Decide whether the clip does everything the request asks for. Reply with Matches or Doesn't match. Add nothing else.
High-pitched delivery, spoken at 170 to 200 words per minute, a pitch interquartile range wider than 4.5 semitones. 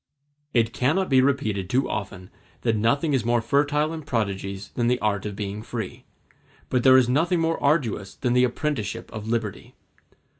Doesn't match